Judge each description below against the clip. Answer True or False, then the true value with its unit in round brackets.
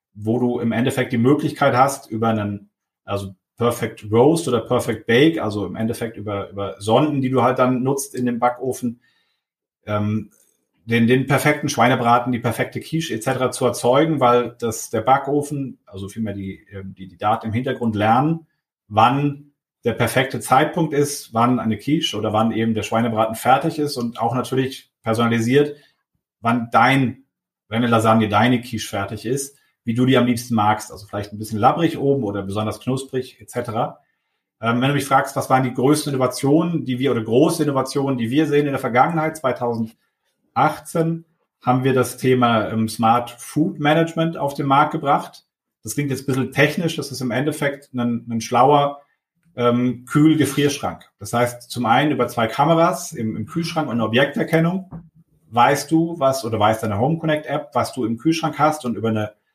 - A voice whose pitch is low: True (125 Hz)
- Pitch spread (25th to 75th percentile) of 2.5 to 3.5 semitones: False (4.0 semitones)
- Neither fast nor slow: True (175 wpm)